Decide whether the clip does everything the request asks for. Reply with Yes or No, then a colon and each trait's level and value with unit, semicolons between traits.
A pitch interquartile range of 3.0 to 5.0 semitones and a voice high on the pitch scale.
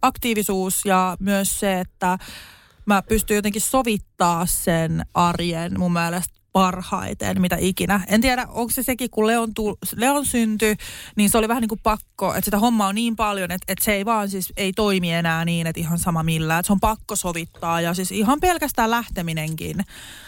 Yes: average, 3.7 semitones; high, 195 Hz